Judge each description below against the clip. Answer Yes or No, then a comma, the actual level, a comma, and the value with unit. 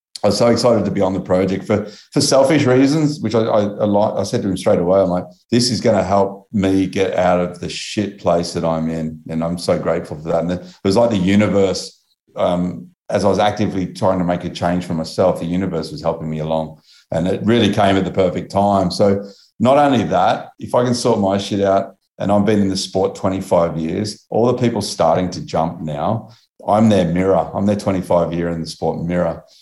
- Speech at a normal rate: No, fast, 235 wpm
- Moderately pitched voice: No, very low, 95 Hz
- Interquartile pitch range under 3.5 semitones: Yes, average, 2.9 semitones